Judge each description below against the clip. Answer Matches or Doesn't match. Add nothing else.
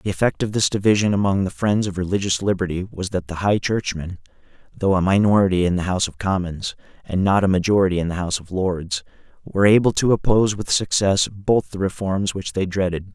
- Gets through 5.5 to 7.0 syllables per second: Matches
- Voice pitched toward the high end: Doesn't match